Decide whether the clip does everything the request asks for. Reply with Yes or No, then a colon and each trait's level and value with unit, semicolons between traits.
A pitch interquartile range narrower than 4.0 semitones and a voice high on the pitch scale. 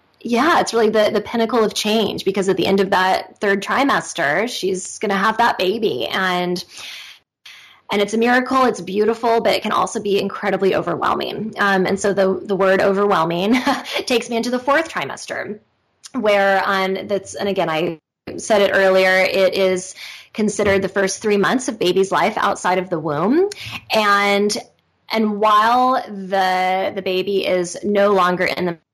Yes: average, 2.8 semitones; high, 200 Hz